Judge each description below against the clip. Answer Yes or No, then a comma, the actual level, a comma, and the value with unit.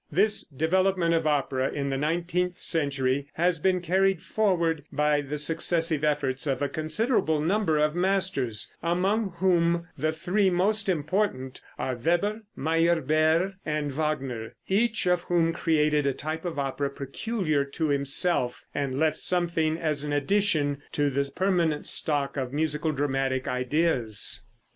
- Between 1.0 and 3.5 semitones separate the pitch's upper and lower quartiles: No, average, 3.9 semitones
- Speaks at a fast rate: No, average, 140 wpm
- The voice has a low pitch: No, medium, 155 Hz